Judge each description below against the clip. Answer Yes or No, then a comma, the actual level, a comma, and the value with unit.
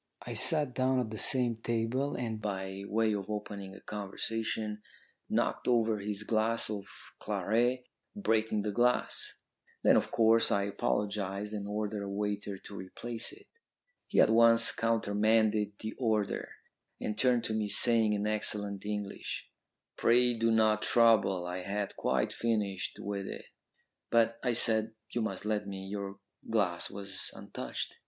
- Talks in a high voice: No, low, 110 Hz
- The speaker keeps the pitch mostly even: Yes, narrow, 2.2 semitones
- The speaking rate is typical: Yes, average, 150 wpm